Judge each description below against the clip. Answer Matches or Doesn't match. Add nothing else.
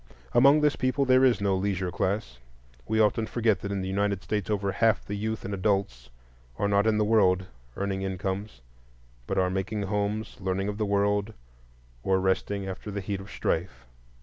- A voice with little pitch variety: Matches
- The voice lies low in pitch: Matches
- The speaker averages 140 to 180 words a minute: Doesn't match